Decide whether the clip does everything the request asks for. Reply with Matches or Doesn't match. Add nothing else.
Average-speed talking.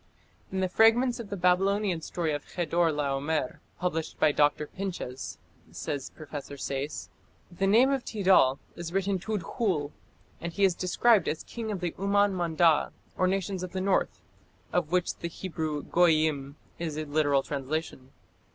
Matches